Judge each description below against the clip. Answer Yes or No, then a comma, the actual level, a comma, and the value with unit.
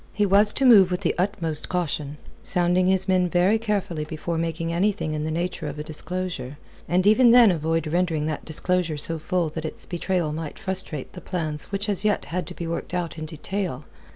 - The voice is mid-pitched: Yes, medium, 175 Hz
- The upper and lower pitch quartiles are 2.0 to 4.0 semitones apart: Yes, average, 3.1 semitones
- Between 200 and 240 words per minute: Yes, fast, 205 wpm